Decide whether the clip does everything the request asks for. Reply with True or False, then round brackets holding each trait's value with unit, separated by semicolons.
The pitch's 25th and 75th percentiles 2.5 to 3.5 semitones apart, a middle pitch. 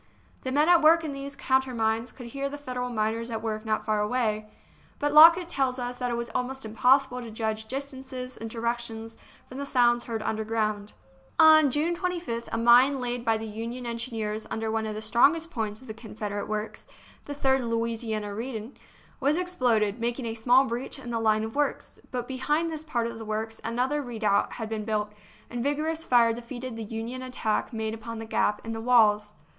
False (3.1 semitones; 235 Hz)